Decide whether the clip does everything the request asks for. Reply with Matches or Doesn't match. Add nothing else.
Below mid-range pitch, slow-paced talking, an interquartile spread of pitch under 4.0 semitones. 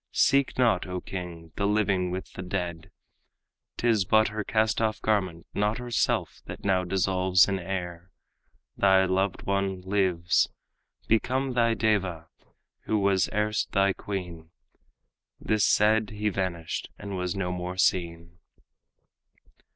Matches